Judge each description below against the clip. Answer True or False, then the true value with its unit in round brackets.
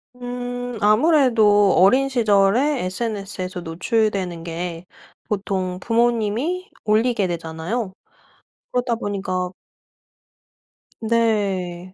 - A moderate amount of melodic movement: True (4.6 semitones)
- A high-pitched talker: True (210 Hz)